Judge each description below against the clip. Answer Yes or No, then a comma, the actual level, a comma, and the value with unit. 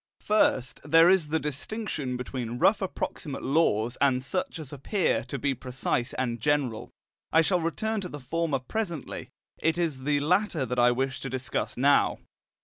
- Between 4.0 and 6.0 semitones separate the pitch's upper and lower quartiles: Yes, average, 4.7 semitones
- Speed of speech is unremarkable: Yes, average, 165 wpm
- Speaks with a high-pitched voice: No, medium, 145 Hz